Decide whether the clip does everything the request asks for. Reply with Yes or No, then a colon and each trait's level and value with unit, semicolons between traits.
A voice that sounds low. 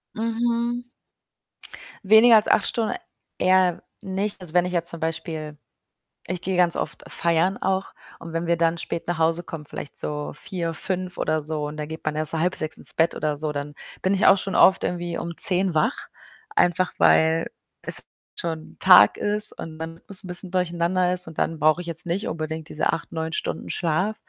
No: medium, 170 Hz